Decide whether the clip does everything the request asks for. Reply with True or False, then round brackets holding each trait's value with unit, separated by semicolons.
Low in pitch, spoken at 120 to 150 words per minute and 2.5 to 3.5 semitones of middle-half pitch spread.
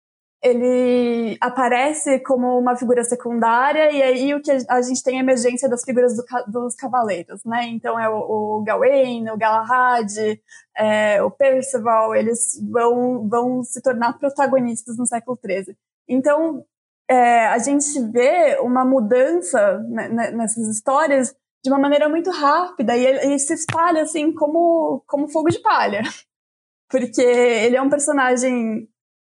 False (250 Hz; 145 wpm; 2.8 semitones)